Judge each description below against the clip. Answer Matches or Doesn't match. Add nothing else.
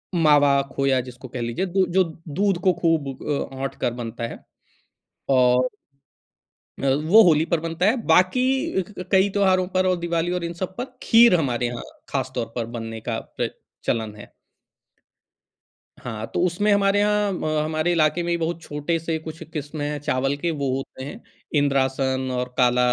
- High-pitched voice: Doesn't match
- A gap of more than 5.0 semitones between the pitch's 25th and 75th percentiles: Matches